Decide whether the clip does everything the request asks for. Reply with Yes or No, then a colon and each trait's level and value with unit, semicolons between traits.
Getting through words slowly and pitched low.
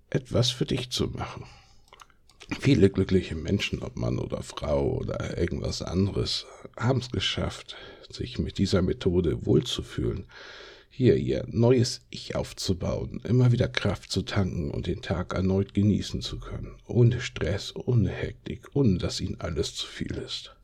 No: average, 150 wpm; low, 100 Hz